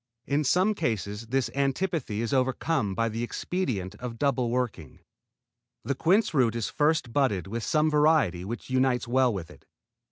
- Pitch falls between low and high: No, low, 125 Hz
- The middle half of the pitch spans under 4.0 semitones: No, average, 4.6 semitones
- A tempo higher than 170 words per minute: No, average, 160 wpm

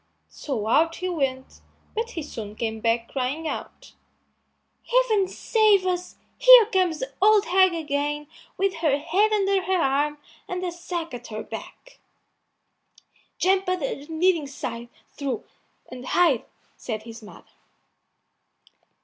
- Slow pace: Yes, slow, 130 wpm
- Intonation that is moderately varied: No, wide, 6.1 semitones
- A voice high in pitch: Yes, very high, 325 Hz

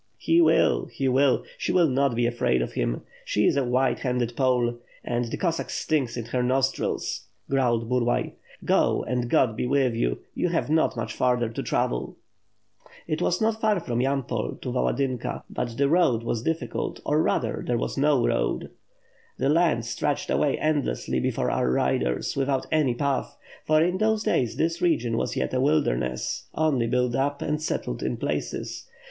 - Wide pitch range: No, average, 4.3 semitones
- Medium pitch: No, low, 130 Hz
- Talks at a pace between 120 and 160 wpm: No, average, 180 wpm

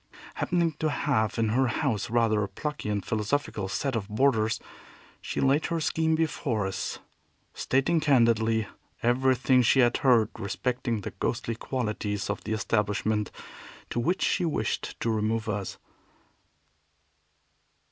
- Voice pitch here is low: Yes, low, 115 Hz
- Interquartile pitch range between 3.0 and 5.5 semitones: Yes, average, 4.1 semitones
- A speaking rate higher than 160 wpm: No, slow, 135 wpm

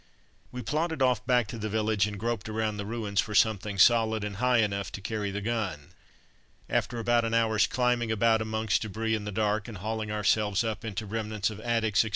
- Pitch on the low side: Yes, low, 110 Hz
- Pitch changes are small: Yes, narrow, 1.8 semitones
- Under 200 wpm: No, fast, 205 wpm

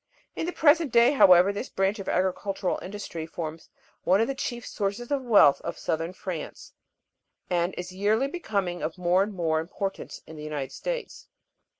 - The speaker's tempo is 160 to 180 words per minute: Yes, average, 175 wpm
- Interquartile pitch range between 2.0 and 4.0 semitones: No, average, 5.1 semitones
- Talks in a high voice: Yes, high, 195 Hz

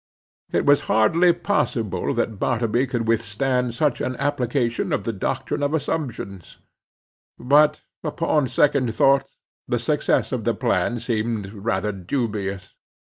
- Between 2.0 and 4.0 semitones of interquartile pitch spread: No, average, 4.5 semitones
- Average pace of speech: No, slow, 130 wpm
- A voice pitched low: Yes, low, 120 Hz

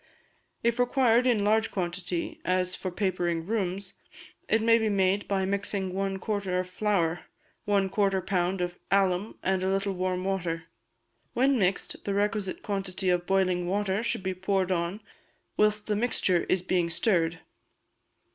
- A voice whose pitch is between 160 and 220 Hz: Yes, high, 190 Hz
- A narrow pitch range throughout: Yes, narrow, 2.2 semitones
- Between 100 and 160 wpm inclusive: Yes, average, 155 wpm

